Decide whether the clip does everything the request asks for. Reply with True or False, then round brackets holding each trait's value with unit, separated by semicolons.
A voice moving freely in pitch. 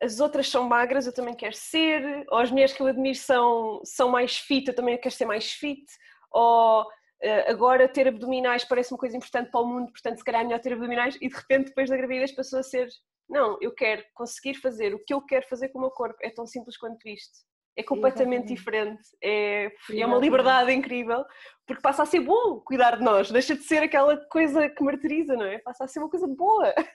False (2.4 semitones)